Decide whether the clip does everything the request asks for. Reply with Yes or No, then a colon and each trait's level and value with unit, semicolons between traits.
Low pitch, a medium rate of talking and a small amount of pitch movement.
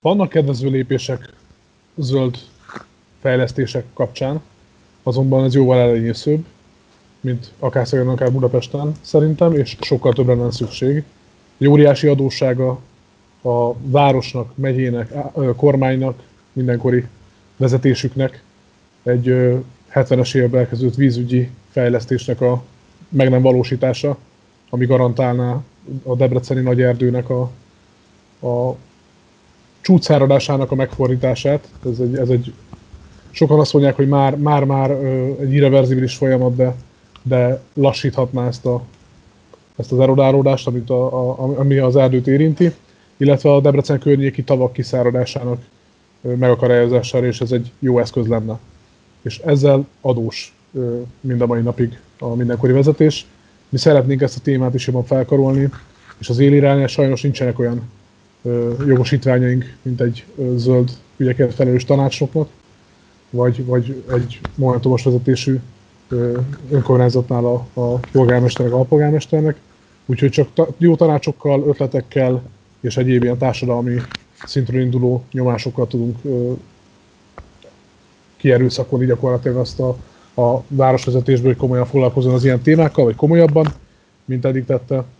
Yes: low, 130 Hz; average, 115 wpm; narrow, 1.8 semitones